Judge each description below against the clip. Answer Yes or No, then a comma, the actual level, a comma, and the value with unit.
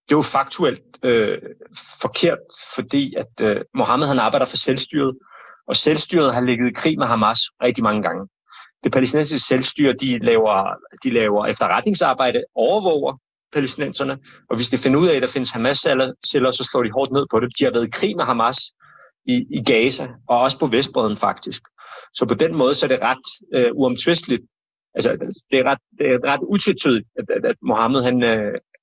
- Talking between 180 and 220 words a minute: Yes, average, 185 wpm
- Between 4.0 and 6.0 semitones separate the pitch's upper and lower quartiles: No, average, 3.5 semitones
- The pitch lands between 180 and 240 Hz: No, low, 135 Hz